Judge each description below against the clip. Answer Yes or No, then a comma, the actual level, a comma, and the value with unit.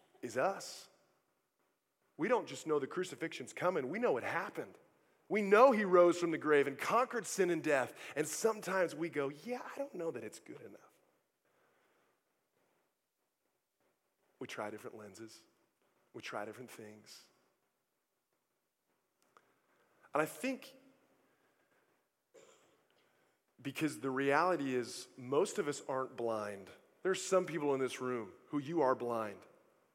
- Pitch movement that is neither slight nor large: No, wide, 8.7 semitones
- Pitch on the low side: No, medium, 160 Hz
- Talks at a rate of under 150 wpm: Yes, slow, 135 wpm